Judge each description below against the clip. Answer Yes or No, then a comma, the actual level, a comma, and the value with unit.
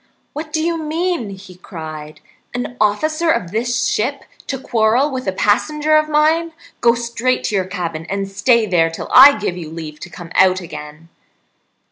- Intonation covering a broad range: Yes, wide, 8.3 semitones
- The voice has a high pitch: Yes, high, 220 Hz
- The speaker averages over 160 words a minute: Yes, average, 175 wpm